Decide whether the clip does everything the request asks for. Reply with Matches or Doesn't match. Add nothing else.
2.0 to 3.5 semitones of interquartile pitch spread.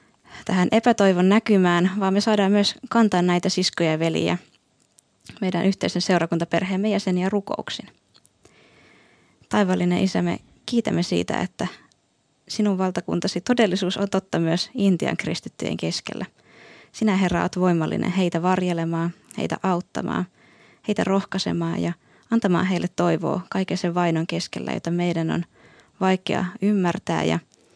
Matches